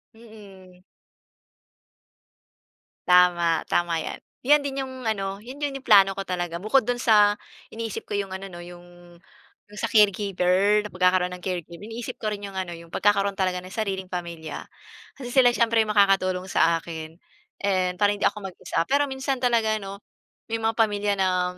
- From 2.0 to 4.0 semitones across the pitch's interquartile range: Yes, average, 3.6 semitones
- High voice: Yes, high, 195 Hz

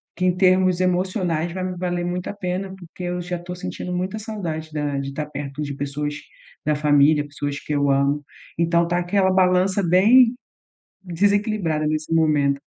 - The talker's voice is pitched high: No, medium, 175 Hz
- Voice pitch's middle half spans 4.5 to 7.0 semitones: No, average, 3.7 semitones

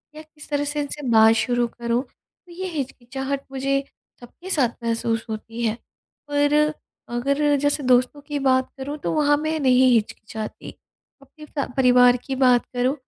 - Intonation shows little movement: No, average, 3.1 semitones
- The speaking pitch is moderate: No, very high, 265 Hz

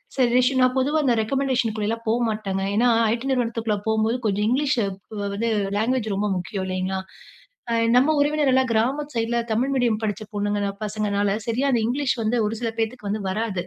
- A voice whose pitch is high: Yes, high, 225 Hz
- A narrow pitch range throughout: No, average, 3.4 semitones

